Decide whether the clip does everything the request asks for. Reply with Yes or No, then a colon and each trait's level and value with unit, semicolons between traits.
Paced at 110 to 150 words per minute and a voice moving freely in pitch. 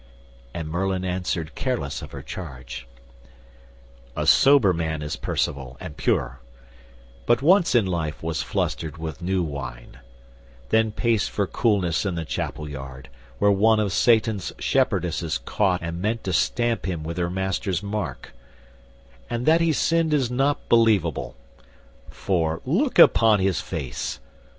Yes: average, 140 wpm; wide, 5.9 semitones